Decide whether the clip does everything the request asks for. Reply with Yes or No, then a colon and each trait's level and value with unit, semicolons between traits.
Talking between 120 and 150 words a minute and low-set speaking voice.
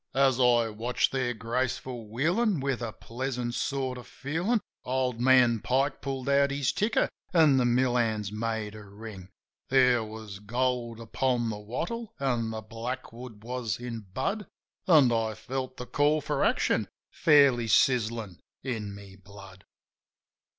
Yes: average, 145 wpm; low, 125 Hz